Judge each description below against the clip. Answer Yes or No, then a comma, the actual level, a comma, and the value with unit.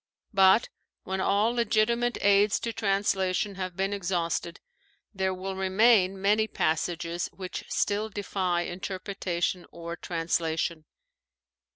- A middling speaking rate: No, slow, 105 wpm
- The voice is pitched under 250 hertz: Yes, high, 190 Hz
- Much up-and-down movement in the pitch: No, narrow, 2.6 semitones